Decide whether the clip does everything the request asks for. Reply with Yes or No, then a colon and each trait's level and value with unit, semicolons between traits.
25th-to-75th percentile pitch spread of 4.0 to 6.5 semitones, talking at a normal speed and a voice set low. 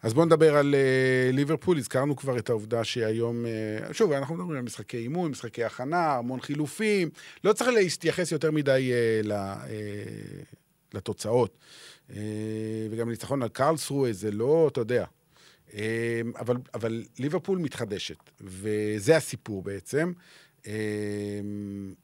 Yes: wide, 5.5 semitones; average, 135 wpm; low, 120 Hz